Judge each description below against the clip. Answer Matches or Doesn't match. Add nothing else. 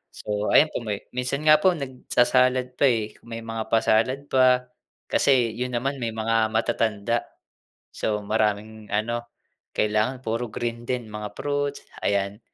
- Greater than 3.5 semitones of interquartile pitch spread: Doesn't match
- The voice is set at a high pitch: Doesn't match